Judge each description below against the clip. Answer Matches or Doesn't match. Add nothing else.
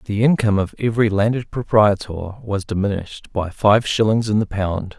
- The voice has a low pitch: Matches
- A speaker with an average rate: Matches